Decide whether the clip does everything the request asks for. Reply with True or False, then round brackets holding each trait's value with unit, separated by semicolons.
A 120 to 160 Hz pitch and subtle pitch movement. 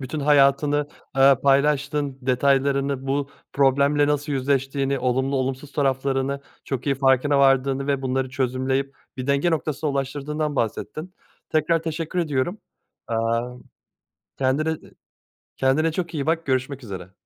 True (140 Hz; 1.8 semitones)